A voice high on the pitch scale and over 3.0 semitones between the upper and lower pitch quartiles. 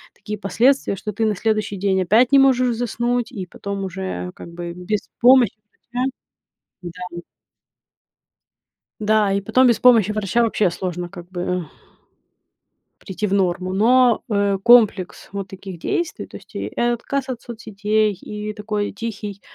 Yes: high, 210 Hz; average, 3.8 semitones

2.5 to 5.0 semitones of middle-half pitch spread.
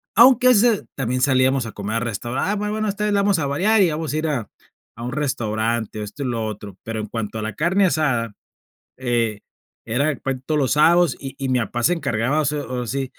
No: wide, 5.6 semitones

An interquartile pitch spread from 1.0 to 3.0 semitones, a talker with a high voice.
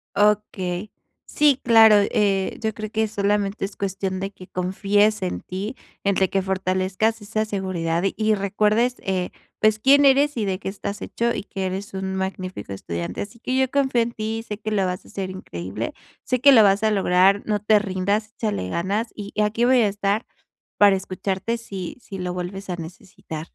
Yes: narrow, 2.5 semitones; high, 200 Hz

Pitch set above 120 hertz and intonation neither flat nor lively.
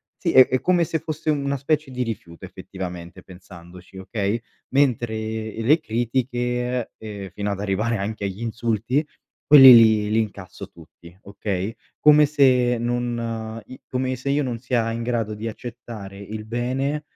No: low, 115 Hz; average, 3.7 semitones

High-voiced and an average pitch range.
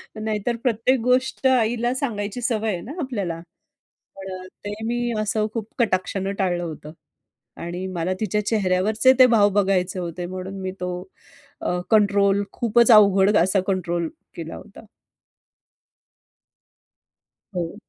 Yes: high, 205 Hz; average, 3.6 semitones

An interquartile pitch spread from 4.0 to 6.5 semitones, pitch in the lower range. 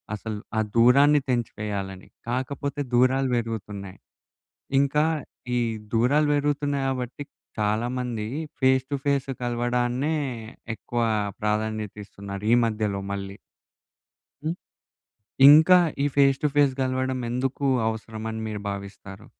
Yes: average, 4.3 semitones; low, 120 Hz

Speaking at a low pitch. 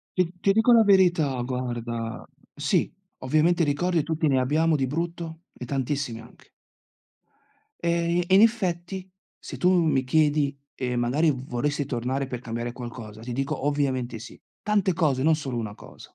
No: medium, 145 Hz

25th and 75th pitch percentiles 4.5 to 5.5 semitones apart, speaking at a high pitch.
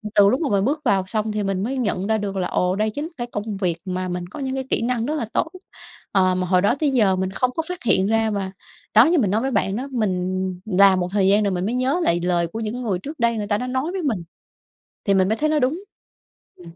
Yes: average, 5.1 semitones; high, 210 Hz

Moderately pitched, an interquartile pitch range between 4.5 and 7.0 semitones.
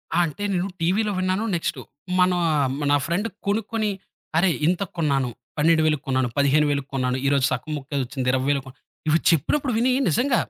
Yes: medium, 155 Hz; wide, 5.4 semitones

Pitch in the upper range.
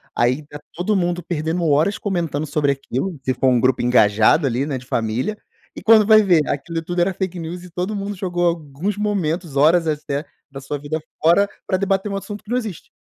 No: medium, 165 Hz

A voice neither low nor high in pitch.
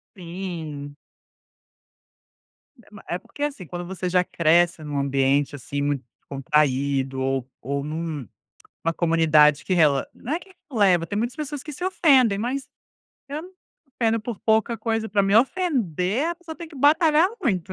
Yes: medium, 180 Hz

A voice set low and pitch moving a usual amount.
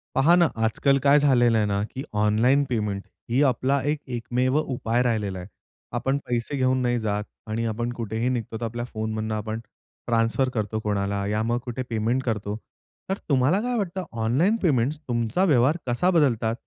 Yes: low, 120 Hz; average, 3.5 semitones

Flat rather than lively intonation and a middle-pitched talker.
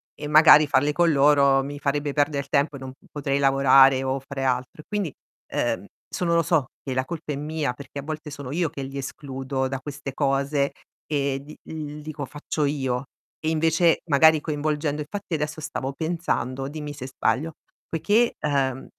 Yes: narrow, 2.3 semitones; medium, 145 Hz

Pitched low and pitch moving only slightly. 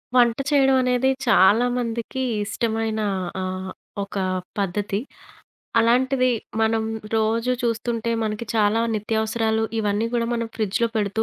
No: high, 225 Hz; narrow, 1.9 semitones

